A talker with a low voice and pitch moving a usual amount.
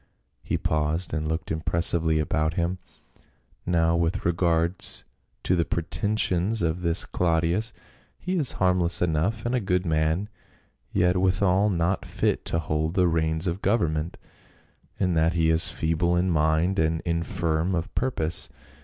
No: very low, 85 Hz; narrow, 2.3 semitones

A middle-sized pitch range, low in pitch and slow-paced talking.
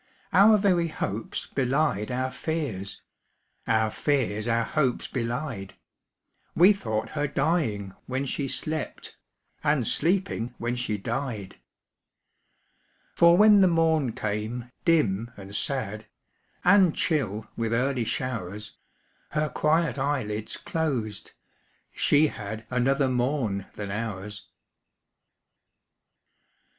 No: wide, 6.0 semitones; low, 125 Hz; slow, 105 wpm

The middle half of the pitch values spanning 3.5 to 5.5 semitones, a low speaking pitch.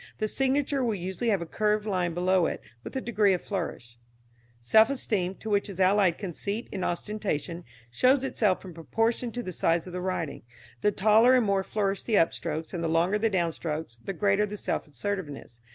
No: average, 4.0 semitones; high, 195 Hz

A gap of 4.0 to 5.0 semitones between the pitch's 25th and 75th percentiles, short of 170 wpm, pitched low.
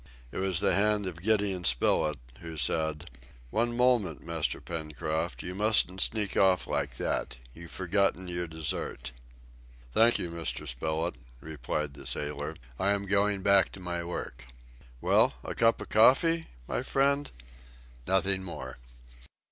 Yes: average, 4.3 semitones; average, 140 wpm; very low, 90 Hz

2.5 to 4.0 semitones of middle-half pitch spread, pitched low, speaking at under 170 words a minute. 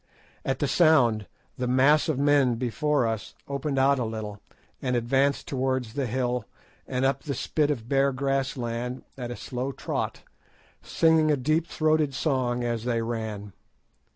Yes: average, 2.9 semitones; low, 130 Hz; average, 160 wpm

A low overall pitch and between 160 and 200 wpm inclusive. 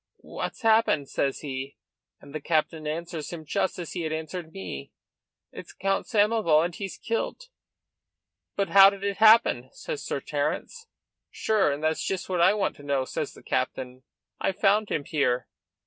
No: medium, 170 Hz; average, 170 wpm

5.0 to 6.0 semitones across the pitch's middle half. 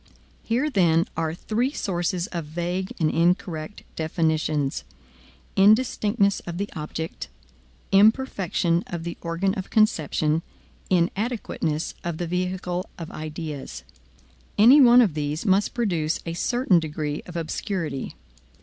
No: average, 4.0 semitones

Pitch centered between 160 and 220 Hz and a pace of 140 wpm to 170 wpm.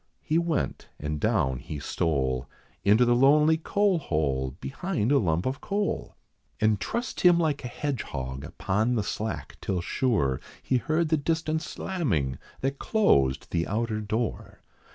No: low, 115 Hz; average, 150 wpm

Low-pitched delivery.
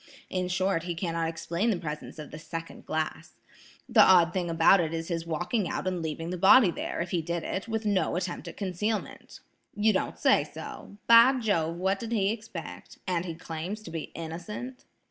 No: medium, 180 Hz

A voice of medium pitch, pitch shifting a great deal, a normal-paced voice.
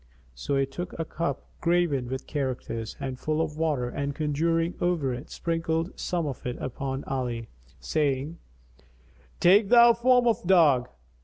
No: medium, 150 Hz; average, 4.3 semitones; average, 150 wpm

